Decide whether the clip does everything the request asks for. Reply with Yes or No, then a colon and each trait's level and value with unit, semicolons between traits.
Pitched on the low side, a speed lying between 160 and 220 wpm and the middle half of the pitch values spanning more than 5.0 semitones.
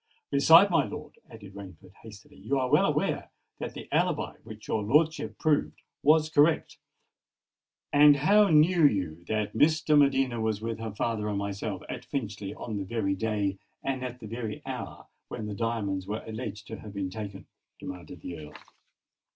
Yes: low, 110 Hz; average, 175 wpm; wide, 5.5 semitones